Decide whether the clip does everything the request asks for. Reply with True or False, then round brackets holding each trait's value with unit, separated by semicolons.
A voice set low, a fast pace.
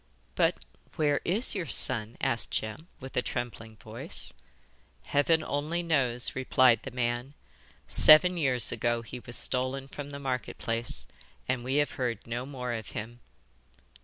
False (130 Hz; 150 wpm)